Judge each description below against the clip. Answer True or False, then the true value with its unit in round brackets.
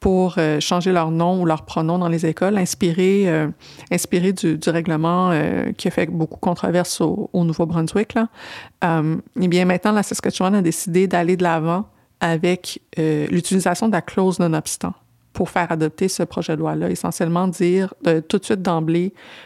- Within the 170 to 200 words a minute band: True (180 wpm)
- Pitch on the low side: False (175 Hz)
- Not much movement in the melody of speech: True (2.2 semitones)